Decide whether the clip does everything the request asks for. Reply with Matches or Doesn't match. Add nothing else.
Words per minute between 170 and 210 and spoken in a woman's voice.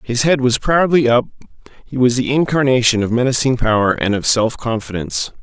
Doesn't match